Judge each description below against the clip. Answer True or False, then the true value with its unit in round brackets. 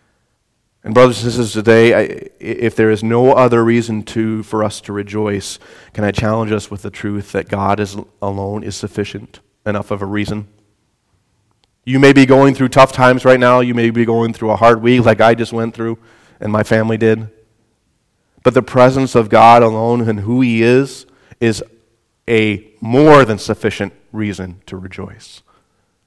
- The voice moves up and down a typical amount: False (2.1 semitones)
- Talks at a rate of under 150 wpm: False (180 wpm)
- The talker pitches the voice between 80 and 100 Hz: False (110 Hz)